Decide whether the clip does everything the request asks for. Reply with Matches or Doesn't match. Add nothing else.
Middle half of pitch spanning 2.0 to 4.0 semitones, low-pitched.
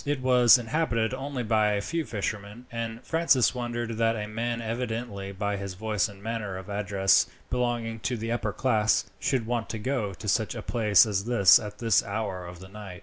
Matches